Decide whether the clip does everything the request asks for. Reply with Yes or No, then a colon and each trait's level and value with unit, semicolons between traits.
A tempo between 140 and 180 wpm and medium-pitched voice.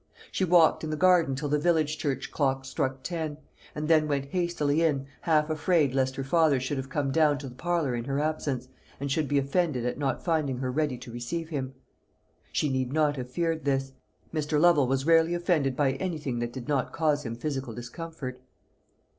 No: average, 200 wpm; medium, 145 Hz